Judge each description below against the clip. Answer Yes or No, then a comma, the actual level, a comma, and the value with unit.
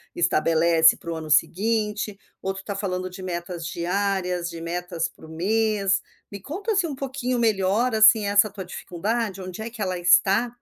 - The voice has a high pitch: Yes, high, 195 Hz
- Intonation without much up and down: No, average, 3.8 semitones